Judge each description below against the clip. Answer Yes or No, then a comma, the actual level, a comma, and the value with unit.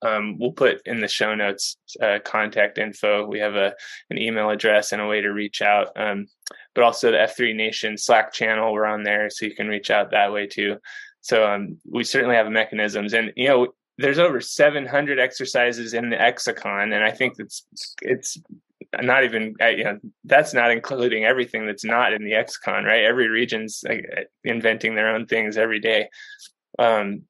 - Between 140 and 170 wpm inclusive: No, average, 190 wpm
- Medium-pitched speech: No, low, 110 Hz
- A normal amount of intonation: No, narrow, 2.3 semitones